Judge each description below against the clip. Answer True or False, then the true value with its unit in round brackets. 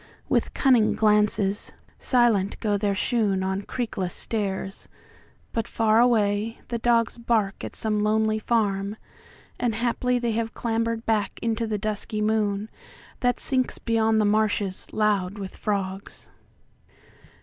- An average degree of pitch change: False (2.1 semitones)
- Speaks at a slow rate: True (115 wpm)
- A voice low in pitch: False (215 Hz)